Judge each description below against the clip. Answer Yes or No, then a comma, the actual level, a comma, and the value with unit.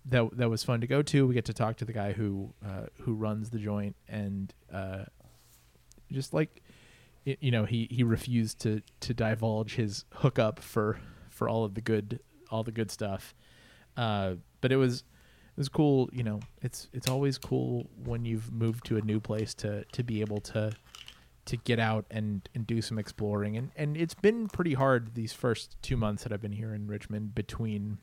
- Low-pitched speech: Yes, low, 115 Hz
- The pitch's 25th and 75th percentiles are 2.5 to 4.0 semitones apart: Yes, average, 2.8 semitones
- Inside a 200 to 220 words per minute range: Yes, fast, 205 wpm